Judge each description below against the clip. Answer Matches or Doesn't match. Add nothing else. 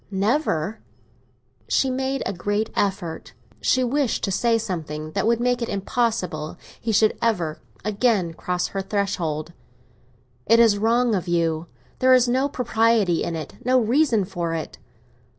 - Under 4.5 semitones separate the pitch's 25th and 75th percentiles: Doesn't match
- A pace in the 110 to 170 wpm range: Matches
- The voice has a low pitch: Doesn't match